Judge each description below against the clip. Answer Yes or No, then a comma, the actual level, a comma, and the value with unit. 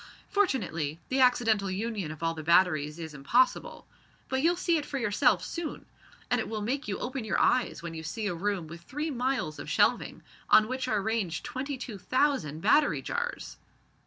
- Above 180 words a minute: Yes, average, 190 wpm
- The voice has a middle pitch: No, high, 220 Hz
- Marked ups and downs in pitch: Yes, wide, 7.7 semitones